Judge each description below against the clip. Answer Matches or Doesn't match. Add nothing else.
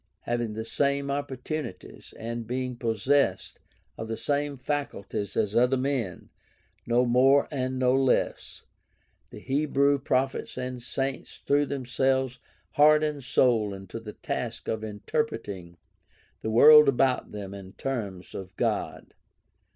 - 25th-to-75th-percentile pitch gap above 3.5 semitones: Matches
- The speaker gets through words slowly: Matches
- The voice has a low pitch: Matches